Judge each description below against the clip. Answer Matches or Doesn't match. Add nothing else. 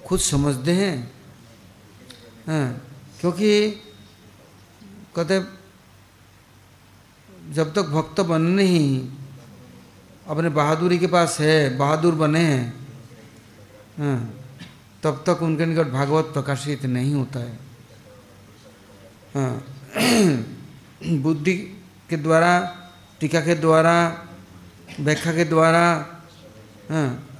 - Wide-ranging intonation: Matches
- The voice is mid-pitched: Matches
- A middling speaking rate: Doesn't match